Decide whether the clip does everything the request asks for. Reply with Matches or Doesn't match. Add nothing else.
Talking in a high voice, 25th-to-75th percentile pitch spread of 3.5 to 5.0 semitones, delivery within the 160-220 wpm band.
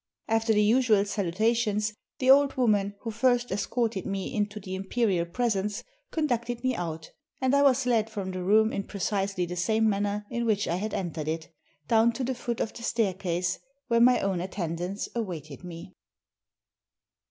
Matches